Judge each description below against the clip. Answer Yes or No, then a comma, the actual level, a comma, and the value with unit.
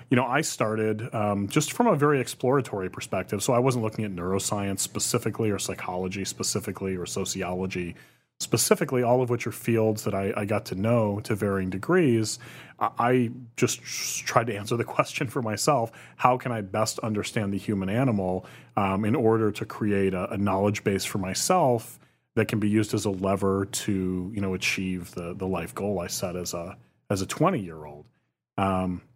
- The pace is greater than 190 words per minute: No, average, 185 wpm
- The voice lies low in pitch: Yes, low, 105 Hz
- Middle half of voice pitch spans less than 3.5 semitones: No, average, 3.8 semitones